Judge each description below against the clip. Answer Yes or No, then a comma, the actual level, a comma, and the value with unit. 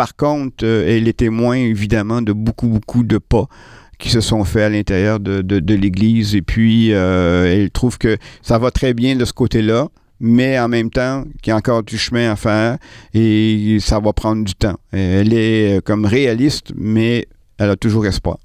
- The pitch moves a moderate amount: No, narrow, 2.2 semitones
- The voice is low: Yes, low, 110 Hz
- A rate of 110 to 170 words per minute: No, average, 200 wpm